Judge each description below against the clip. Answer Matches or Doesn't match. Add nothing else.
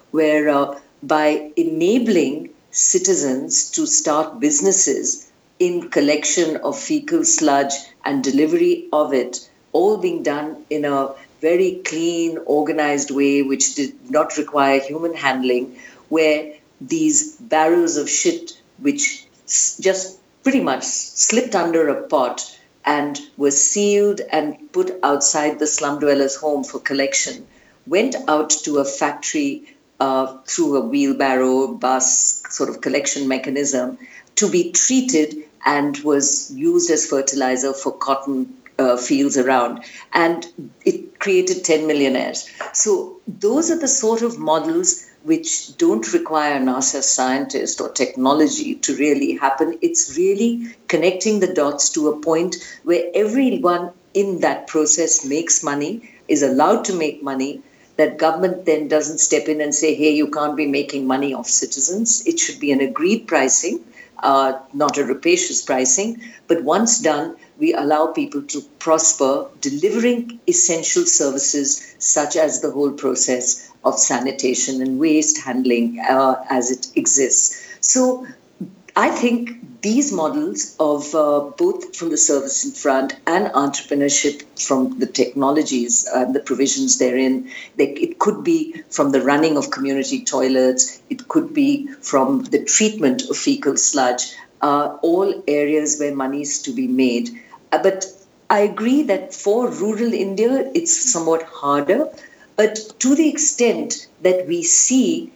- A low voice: Doesn't match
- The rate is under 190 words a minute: Matches